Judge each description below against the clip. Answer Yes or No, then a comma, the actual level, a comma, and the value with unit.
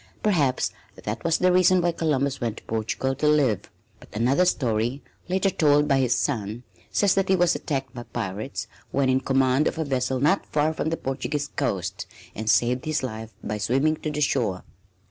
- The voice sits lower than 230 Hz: Yes, low, 135 Hz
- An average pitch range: Yes, average, 4.5 semitones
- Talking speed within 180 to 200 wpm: Yes, average, 190 wpm